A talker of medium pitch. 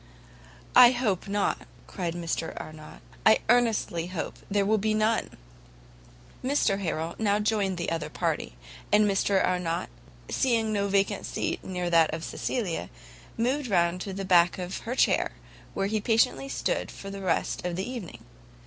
No: high, 195 Hz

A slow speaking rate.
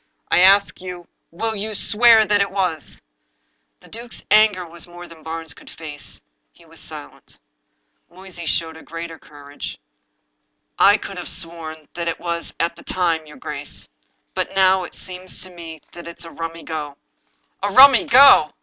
No: average, 170 wpm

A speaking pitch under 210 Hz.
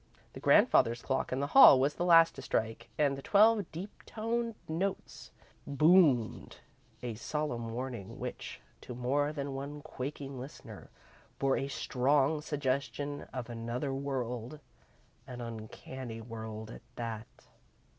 Yes: low, 135 Hz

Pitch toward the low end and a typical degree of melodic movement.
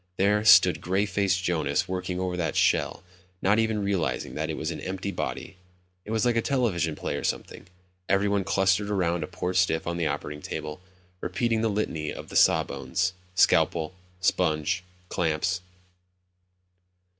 Yes: very low, 90 Hz; average, 3.2 semitones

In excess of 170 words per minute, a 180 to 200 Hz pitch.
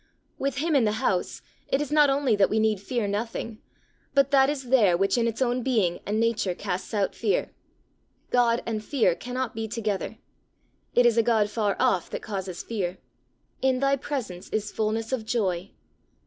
No: average, 185 wpm; high, 225 Hz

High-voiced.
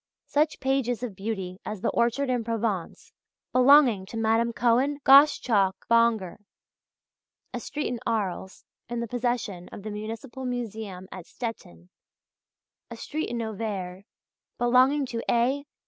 Yes: high, 230 Hz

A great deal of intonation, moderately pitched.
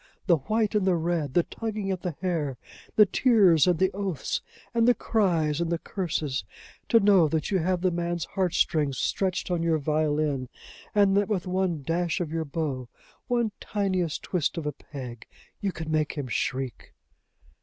No: average, 4.0 semitones; medium, 170 Hz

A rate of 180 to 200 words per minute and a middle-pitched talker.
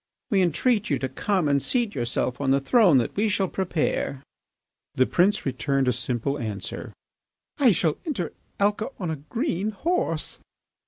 No: average, 160 wpm; medium, 165 Hz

